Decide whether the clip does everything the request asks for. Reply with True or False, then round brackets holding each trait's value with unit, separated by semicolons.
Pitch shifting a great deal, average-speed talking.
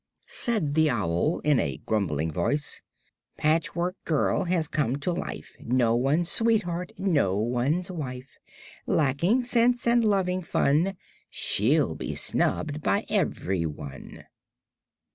False (6.6 semitones; 115 wpm)